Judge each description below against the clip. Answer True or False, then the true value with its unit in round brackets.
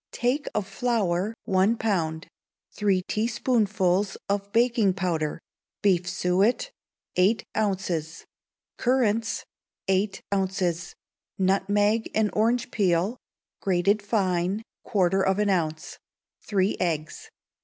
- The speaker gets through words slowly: True (100 wpm)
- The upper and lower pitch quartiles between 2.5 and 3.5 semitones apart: True (3.1 semitones)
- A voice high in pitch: True (195 Hz)